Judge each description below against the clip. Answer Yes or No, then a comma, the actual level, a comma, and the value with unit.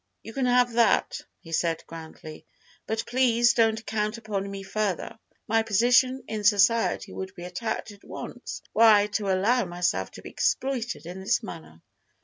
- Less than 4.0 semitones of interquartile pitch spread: Yes, average, 3.6 semitones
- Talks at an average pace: Yes, average, 165 wpm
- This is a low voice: No, high, 215 Hz